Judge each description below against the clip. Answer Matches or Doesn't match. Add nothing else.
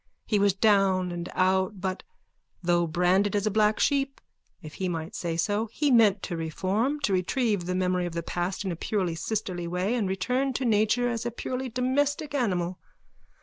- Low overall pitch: Doesn't match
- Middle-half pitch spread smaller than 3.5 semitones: Doesn't match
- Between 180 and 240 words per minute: Matches